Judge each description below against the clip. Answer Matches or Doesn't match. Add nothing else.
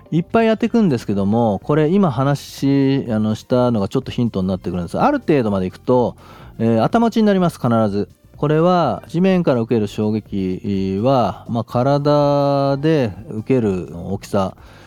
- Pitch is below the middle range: Matches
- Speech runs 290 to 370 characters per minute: Matches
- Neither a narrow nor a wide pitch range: Doesn't match